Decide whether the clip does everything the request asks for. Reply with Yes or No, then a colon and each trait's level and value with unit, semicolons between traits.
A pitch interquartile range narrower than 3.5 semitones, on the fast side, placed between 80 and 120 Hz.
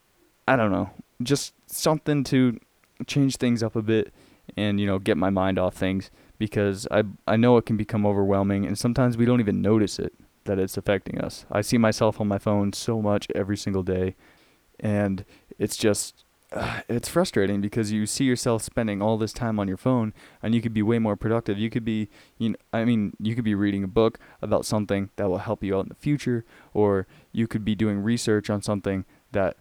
Yes: narrow, 2.4 semitones; fast, 215 wpm; low, 105 Hz